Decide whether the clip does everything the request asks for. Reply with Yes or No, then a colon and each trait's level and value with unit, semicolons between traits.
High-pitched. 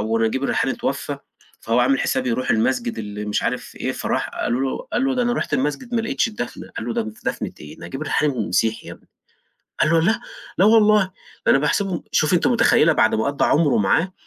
No: medium, 140 Hz